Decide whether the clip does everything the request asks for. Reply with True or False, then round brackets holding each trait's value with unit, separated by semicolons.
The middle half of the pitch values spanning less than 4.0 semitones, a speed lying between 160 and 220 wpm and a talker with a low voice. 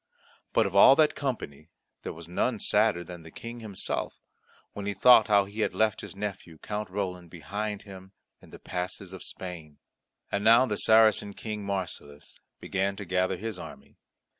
True (3.0 semitones; 175 wpm; 100 Hz)